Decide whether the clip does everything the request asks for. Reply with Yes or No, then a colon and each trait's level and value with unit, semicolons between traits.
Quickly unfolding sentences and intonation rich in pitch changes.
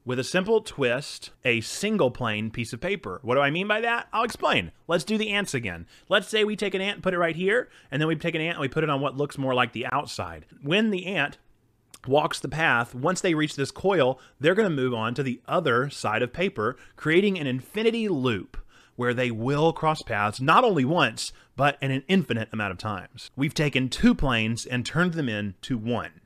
Yes: fast, 230 wpm; wide, 6.9 semitones